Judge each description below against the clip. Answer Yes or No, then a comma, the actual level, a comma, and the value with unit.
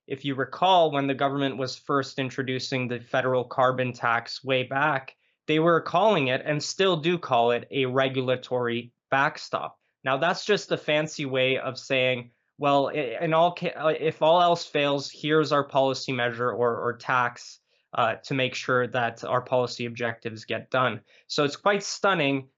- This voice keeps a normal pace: Yes, average, 170 wpm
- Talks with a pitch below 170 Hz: Yes, low, 135 Hz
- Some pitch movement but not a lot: Yes, average, 3.2 semitones